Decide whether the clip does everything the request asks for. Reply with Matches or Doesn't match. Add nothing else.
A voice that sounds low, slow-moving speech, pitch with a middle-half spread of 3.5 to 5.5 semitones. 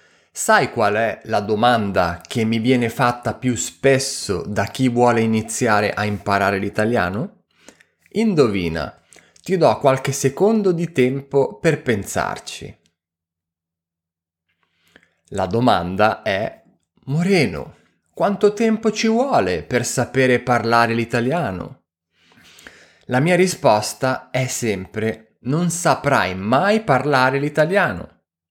Matches